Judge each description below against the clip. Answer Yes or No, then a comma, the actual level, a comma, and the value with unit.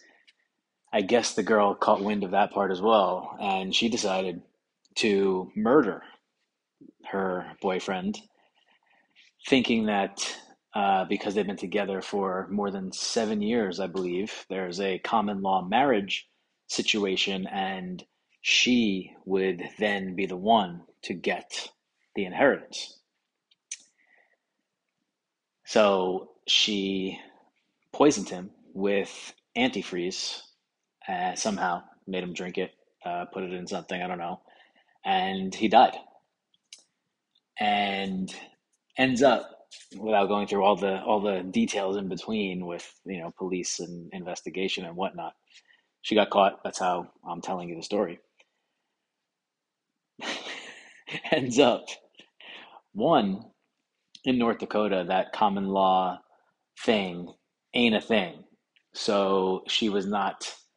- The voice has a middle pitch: No, very low, 95 Hz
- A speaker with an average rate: No, slow, 120 wpm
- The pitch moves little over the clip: Yes, narrow, 1.9 semitones